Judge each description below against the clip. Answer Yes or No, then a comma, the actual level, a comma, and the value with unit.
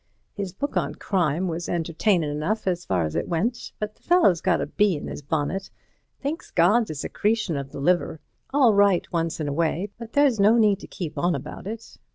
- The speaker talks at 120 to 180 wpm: No, fast, 205 wpm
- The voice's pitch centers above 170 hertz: Yes, medium, 185 Hz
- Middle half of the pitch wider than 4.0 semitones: Yes, average, 4.8 semitones